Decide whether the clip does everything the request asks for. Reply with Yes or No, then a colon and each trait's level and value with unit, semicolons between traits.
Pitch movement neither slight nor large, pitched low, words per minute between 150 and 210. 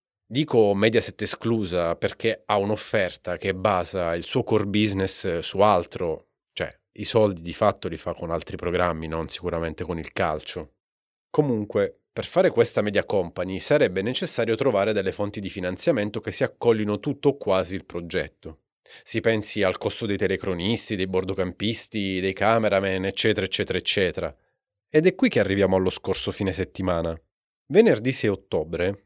Yes: average, 3.0 semitones; low, 100 Hz; average, 155 wpm